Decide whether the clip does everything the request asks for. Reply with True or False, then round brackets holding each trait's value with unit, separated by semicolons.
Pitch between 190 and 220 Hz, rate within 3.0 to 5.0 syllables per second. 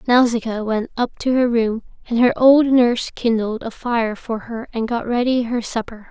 False (235 Hz; 4.8 syllables/s)